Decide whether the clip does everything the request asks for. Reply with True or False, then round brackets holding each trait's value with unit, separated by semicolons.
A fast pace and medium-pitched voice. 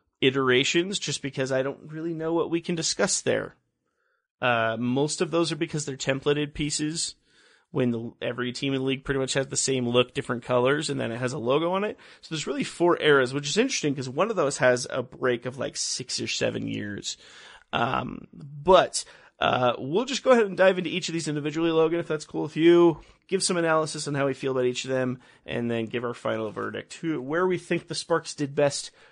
True (225 wpm; 145 Hz)